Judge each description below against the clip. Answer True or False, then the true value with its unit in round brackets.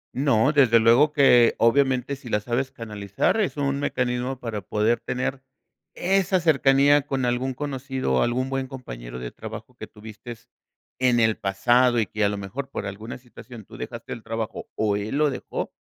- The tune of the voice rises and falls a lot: False (3.7 semitones)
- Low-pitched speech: True (125 Hz)